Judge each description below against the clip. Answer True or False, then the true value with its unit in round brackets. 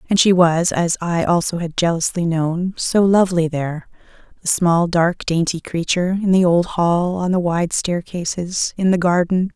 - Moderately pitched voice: True (175 Hz)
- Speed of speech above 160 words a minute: True (175 wpm)